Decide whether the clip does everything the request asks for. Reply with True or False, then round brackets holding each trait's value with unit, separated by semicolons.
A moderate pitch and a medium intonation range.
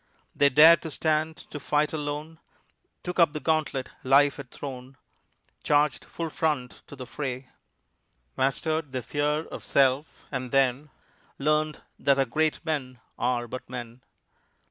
True (145 Hz; 3.0 semitones)